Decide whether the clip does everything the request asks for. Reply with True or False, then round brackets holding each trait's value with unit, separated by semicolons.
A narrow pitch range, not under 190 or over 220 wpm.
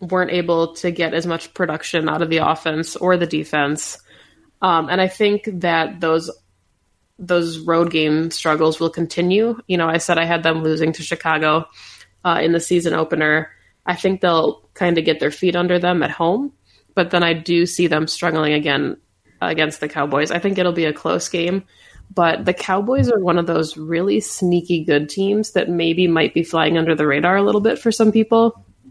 True (2.2 semitones; 200 wpm)